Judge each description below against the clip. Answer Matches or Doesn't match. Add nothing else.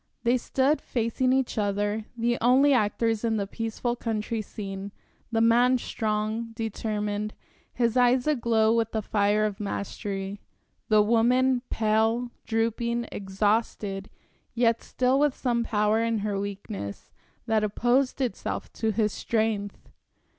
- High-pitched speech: Matches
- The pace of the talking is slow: Matches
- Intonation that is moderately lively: Doesn't match